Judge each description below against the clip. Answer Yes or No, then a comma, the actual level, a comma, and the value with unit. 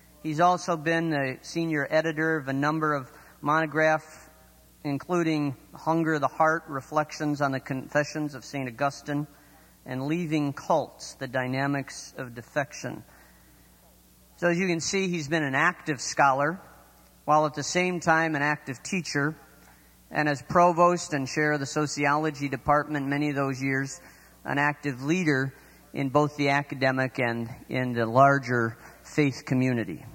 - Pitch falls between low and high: Yes, medium, 145 Hz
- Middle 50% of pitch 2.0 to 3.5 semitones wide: Yes, average, 2.7 semitones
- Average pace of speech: Yes, average, 145 wpm